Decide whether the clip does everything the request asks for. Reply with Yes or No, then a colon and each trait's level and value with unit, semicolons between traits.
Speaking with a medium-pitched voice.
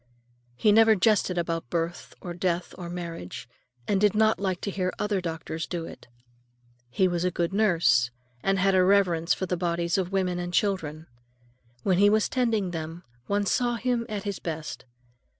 Yes: medium, 180 Hz